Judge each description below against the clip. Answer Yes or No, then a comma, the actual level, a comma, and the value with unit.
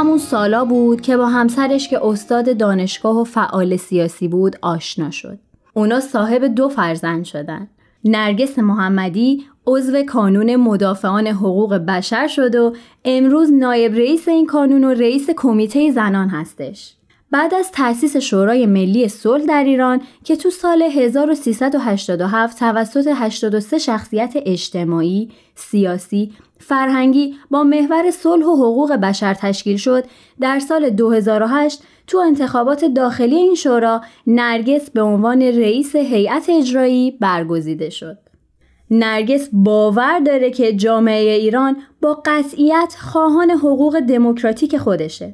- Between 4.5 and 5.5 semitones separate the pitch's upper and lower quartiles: Yes, average, 4.9 semitones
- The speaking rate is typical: Yes, average, 125 wpm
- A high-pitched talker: Yes, high, 240 Hz